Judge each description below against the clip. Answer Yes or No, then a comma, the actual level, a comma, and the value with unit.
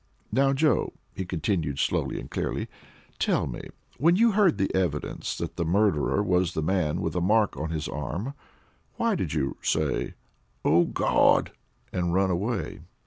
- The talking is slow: No, average, 160 wpm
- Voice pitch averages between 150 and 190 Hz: No, very low, 90 Hz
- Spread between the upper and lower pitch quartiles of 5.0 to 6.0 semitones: Yes, wide, 5.6 semitones